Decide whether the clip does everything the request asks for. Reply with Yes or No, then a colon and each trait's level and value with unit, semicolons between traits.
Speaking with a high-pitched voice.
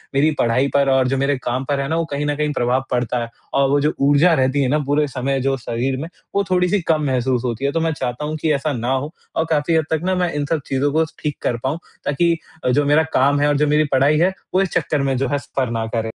No: medium, 140 Hz